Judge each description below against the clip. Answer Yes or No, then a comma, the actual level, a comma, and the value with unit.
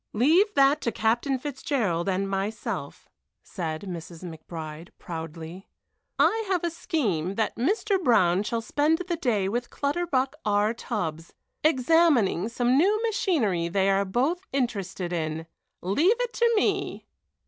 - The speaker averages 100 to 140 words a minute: Yes, slow, 135 wpm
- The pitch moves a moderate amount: No, wide, 8.9 semitones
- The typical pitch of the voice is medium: No, high, 230 Hz